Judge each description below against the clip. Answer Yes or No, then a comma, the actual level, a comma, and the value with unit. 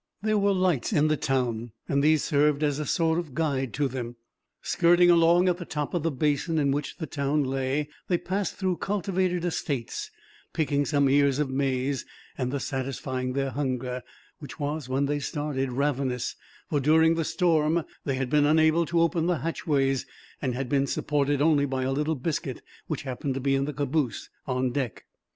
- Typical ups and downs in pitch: Yes, average, 3.2 semitones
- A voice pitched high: No, medium, 145 Hz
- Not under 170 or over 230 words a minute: Yes, average, 185 wpm